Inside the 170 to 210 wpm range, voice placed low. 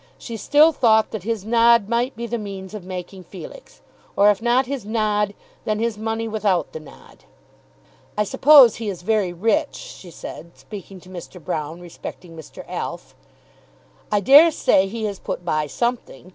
No: average, 175 wpm; high, 210 Hz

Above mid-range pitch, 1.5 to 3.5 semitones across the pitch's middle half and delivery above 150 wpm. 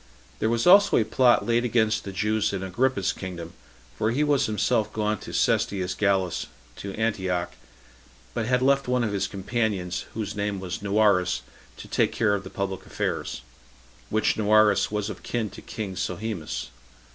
No: low, 105 Hz; average, 3.0 semitones; average, 170 wpm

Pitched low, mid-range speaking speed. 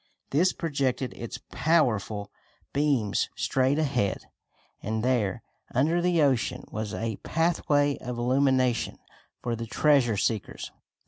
No: low, 130 Hz; slow, 115 wpm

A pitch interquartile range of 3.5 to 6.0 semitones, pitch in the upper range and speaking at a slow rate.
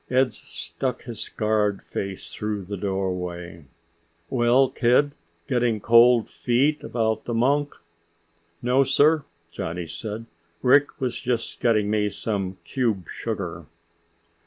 No: average, 3.8 semitones; low, 115 Hz; slow, 115 wpm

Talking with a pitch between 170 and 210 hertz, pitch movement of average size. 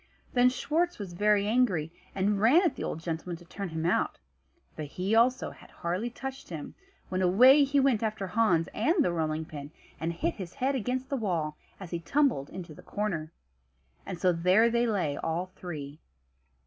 No: high, 190 Hz; wide, 6.6 semitones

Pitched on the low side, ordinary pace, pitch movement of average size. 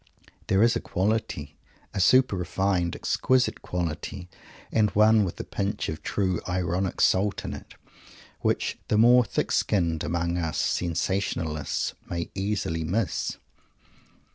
No: very low, 95 Hz; slow, 130 wpm; average, 3.5 semitones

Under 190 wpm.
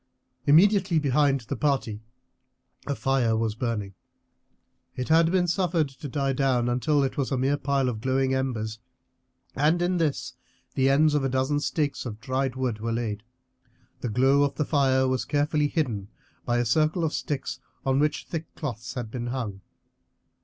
Yes: average, 170 wpm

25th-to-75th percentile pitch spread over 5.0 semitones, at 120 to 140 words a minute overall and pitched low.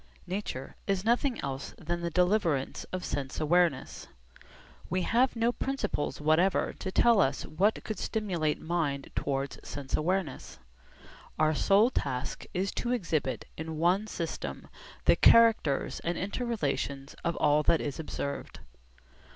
No: wide, 5.6 semitones; slow, 135 wpm; medium, 170 Hz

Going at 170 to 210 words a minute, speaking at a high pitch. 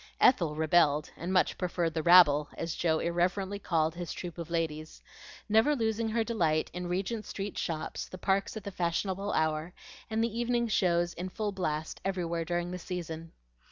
No: average, 175 wpm; medium, 175 Hz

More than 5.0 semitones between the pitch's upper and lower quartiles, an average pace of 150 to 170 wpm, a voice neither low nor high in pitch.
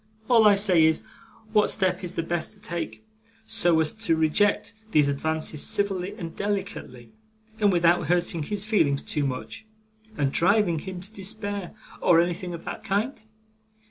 No: average, 4.2 semitones; average, 160 wpm; medium, 180 Hz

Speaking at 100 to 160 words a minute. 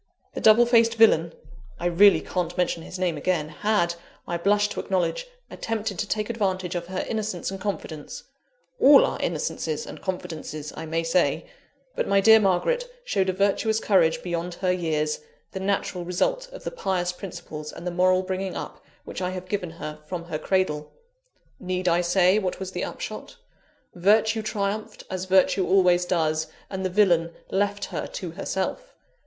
No: average, 170 wpm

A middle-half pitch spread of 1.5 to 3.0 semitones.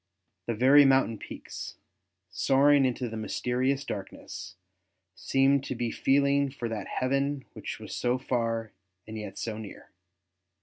No: average, 3.4 semitones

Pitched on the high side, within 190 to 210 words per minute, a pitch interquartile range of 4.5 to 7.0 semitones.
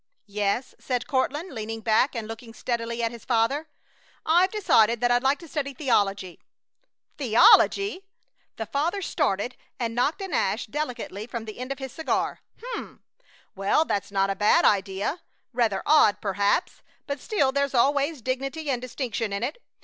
No: high, 245 Hz; average, 160 wpm; average, 5.0 semitones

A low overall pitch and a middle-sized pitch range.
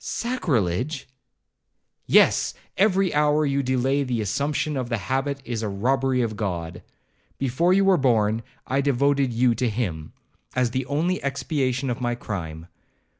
Yes: low, 130 Hz; average, 3.8 semitones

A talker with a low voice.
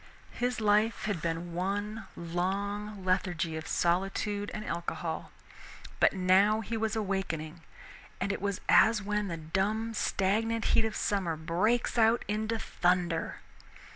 No: high, 200 Hz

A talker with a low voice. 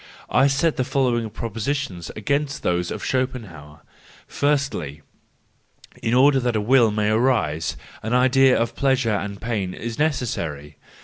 Yes: low, 115 Hz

